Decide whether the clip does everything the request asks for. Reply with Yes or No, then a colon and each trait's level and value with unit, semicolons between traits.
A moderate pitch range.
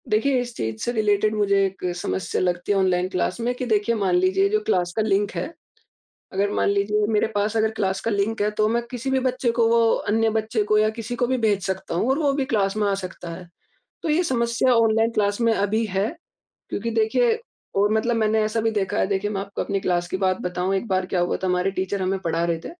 Yes: average, 3.0 semitones